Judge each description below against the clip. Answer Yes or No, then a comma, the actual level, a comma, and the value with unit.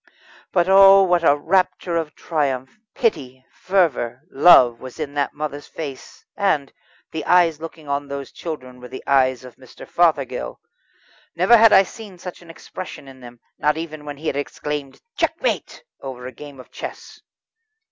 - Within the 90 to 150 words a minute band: No, average, 165 wpm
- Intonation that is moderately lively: Yes, average, 4.8 semitones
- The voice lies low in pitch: No, medium, 150 Hz